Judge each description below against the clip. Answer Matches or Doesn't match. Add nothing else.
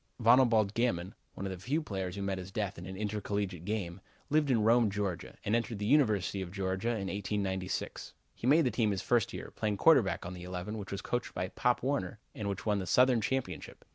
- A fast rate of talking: Matches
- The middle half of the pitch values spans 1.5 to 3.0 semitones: Doesn't match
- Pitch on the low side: Matches